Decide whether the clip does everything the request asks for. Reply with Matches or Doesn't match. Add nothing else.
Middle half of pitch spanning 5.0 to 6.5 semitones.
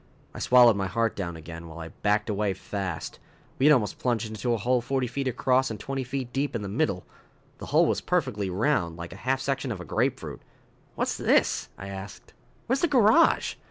Matches